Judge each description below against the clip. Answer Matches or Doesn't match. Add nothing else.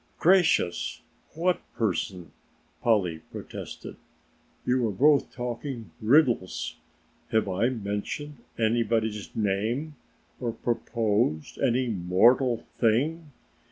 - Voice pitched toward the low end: Matches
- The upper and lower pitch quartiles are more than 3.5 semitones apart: Matches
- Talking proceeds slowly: Matches